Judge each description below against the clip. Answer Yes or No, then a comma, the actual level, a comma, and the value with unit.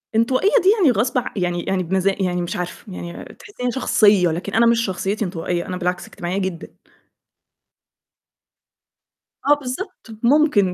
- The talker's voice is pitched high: Yes, high, 195 Hz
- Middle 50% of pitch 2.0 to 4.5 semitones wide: No, wide, 5.6 semitones